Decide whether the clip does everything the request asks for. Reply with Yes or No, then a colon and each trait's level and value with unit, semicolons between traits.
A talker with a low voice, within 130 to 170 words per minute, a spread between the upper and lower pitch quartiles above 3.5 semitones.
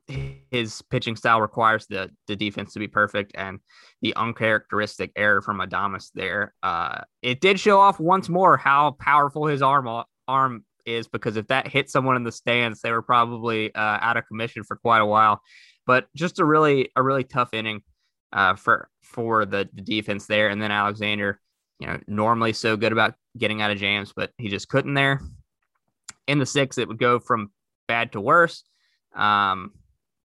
No: low, 115 Hz; average, 185 wpm; average, 4.1 semitones